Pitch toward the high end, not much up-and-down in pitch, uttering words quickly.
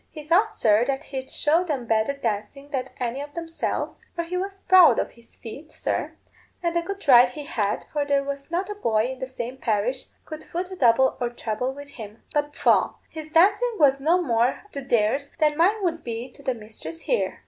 No: very high, 280 Hz; wide, 5.5 semitones; fast, 215 wpm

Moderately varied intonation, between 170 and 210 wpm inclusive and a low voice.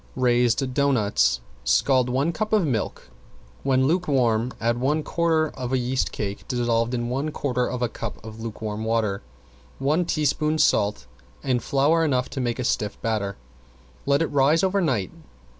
No: average, 4.2 semitones; average, 160 wpm; low, 125 Hz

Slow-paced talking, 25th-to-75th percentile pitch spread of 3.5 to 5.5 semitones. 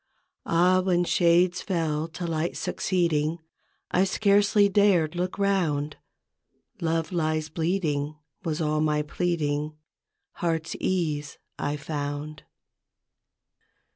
No: slow, 105 wpm; average, 3.0 semitones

